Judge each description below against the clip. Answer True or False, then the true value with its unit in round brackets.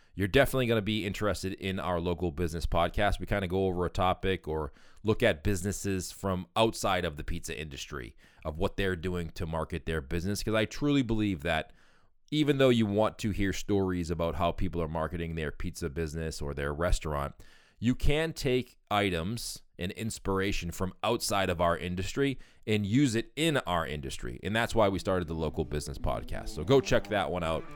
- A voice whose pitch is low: True (95 Hz)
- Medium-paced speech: True (195 wpm)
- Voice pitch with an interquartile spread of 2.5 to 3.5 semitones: False (4.4 semitones)